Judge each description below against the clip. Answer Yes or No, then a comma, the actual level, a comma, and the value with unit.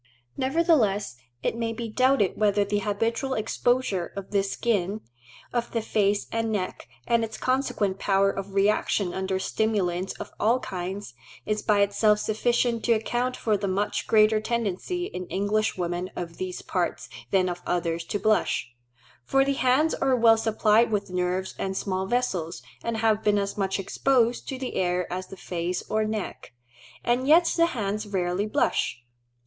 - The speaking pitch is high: Yes, high, 210 Hz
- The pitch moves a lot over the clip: No, average, 3.5 semitones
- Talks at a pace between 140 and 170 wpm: Yes, average, 165 wpm